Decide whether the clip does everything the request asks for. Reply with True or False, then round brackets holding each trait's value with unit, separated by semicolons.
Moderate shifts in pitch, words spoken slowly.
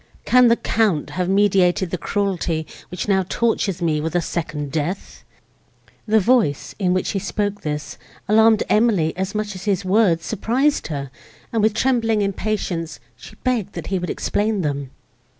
False (4.4 semitones; 165 wpm)